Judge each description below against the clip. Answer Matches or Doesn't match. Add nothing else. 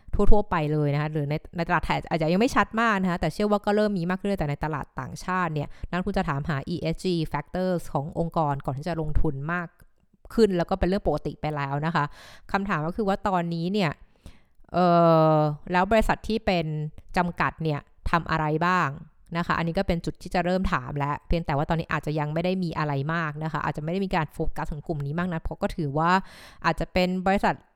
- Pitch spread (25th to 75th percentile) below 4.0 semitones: Matches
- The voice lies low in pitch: Doesn't match